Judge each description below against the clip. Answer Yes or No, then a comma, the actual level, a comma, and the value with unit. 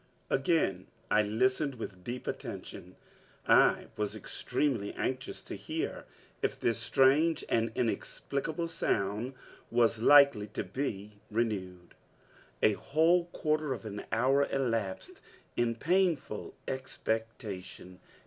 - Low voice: Yes, low, 120 Hz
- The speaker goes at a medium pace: No, slow, 110 wpm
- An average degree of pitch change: Yes, average, 4.8 semitones